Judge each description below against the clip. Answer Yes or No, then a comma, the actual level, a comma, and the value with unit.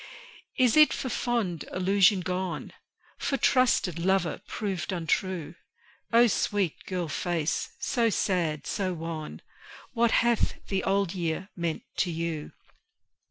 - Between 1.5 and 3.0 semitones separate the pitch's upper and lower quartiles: No, average, 3.7 semitones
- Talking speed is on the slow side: Yes, slow, 120 wpm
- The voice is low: No, medium, 185 Hz